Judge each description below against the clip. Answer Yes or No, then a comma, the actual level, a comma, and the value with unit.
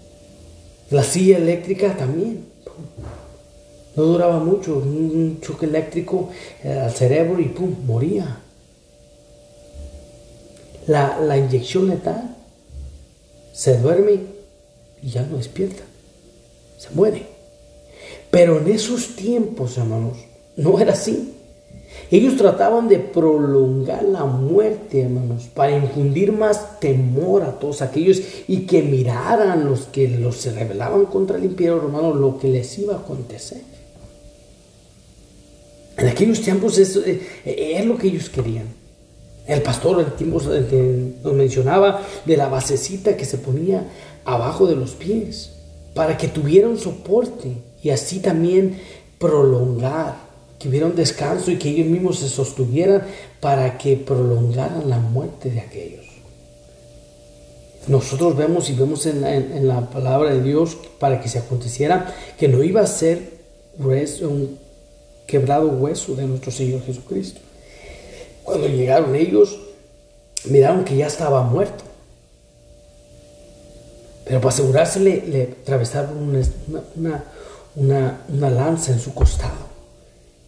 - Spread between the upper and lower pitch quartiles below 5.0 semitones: No, average, 5.3 semitones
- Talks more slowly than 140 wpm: Yes, slow, 125 wpm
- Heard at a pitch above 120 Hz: Yes, medium, 140 Hz